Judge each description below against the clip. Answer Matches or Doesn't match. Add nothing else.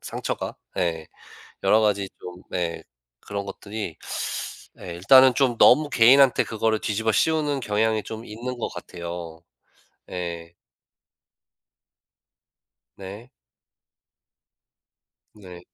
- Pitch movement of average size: Matches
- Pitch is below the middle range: Matches